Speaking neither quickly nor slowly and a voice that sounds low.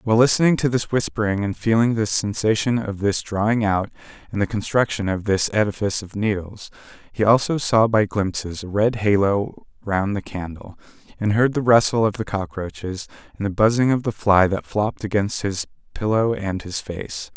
Yes: average, 185 wpm; low, 105 Hz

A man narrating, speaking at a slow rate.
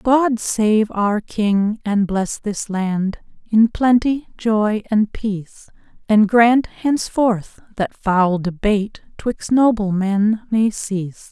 No: female; slow, 120 wpm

